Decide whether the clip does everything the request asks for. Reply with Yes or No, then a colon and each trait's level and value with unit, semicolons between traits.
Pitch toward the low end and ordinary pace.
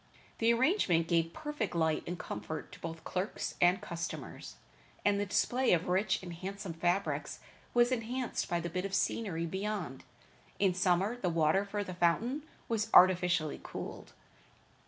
No: medium, 185 Hz; average, 155 wpm